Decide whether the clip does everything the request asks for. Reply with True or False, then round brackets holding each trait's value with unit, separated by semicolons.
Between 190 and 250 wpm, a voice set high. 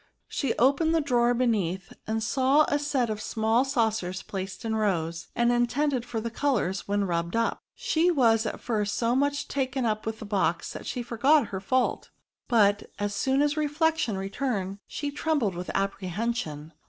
False (175 wpm; 230 Hz)